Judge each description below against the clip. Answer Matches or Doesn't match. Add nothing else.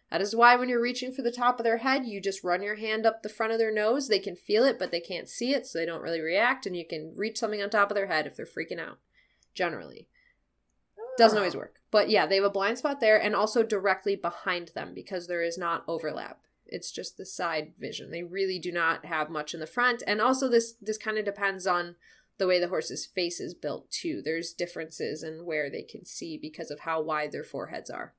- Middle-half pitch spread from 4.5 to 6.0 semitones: Matches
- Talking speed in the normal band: Doesn't match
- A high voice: Matches